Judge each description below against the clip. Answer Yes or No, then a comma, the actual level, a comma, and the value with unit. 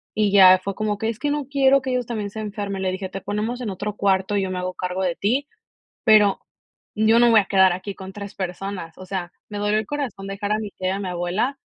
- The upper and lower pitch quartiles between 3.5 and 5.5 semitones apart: No, narrow, 2.4 semitones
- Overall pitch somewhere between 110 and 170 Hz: No, high, 205 Hz